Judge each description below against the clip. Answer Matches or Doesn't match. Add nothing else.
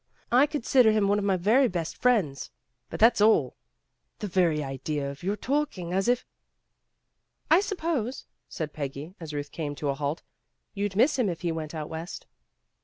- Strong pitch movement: Matches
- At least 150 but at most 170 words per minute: Doesn't match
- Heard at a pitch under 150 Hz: Doesn't match